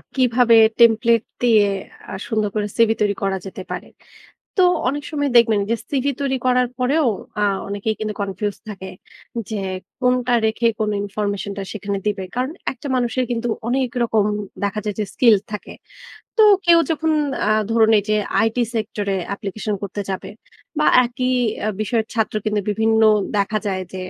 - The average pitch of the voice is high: Yes, high, 220 Hz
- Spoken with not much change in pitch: No, average, 3.4 semitones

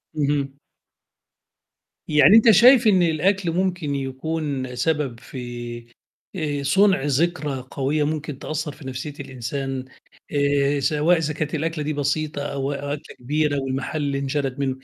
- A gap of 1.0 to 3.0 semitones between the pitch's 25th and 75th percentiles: Yes, narrow, 2.5 semitones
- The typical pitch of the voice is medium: Yes, medium, 145 Hz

